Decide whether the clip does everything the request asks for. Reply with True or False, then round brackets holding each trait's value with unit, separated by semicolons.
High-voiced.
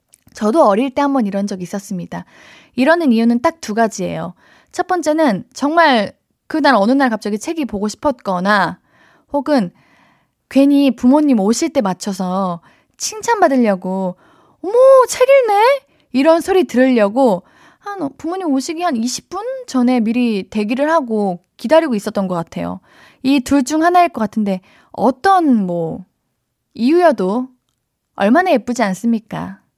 True (260 Hz)